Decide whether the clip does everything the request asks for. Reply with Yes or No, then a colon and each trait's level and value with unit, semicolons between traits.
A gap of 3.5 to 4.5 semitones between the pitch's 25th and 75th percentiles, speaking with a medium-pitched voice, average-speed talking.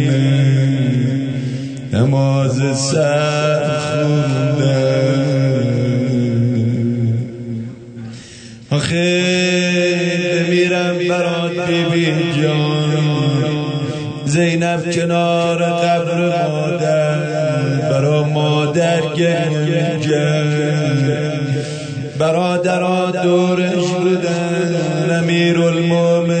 No: average, 3.9 semitones; medium, 150 Hz; slow, 45 wpm